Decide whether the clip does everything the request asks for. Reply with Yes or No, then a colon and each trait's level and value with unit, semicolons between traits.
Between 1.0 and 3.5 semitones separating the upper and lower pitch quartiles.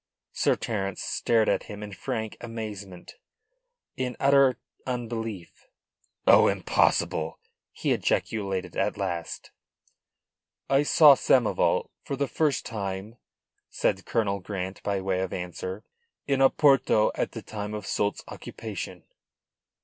No: average, 4.2 semitones